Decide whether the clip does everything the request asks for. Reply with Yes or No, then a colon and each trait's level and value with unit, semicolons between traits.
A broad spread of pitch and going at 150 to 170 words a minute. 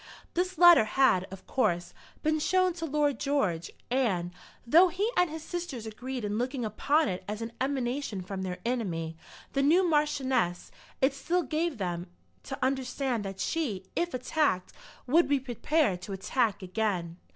Yes: wide, 7.5 semitones; average, 160 wpm